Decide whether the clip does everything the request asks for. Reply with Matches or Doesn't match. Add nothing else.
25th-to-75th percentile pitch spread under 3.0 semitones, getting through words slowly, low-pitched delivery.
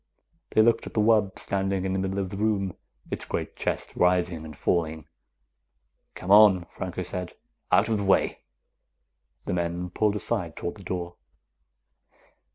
Doesn't match